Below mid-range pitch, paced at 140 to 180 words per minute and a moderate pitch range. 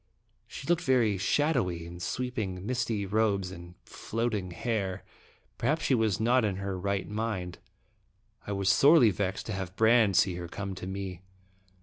Yes: low, 100 Hz; average, 155 wpm; average, 3.8 semitones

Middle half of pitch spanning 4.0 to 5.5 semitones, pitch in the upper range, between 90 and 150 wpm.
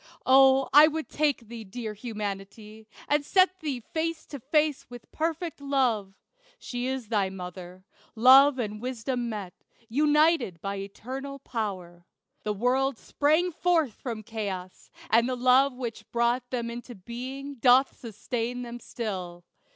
Yes: average, 4.5 semitones; high, 245 Hz; average, 140 wpm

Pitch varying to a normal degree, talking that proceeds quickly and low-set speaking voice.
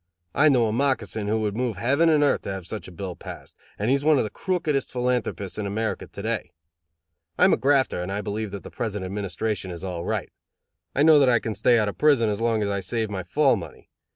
Yes: average, 4.7 semitones; fast, 250 wpm; low, 110 Hz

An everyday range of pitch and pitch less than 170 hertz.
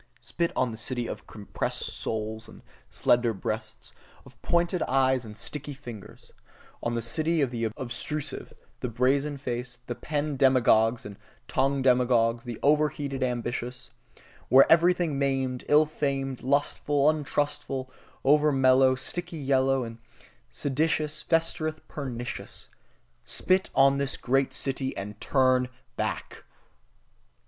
Yes: average, 3.2 semitones; low, 135 Hz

